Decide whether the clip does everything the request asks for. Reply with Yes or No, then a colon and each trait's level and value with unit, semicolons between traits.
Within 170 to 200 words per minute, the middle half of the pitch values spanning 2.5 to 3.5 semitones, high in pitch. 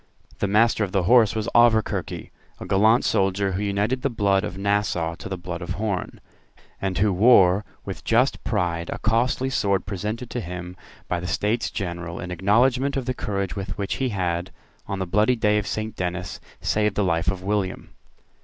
No: average, 190 wpm; average, 3.2 semitones; low, 100 Hz